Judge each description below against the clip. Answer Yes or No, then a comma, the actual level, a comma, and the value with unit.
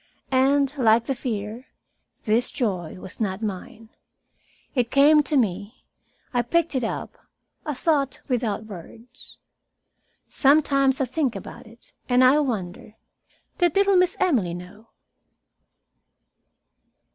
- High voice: Yes, high, 245 Hz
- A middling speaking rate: No, slow, 120 wpm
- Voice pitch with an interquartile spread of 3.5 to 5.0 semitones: Yes, average, 4.5 semitones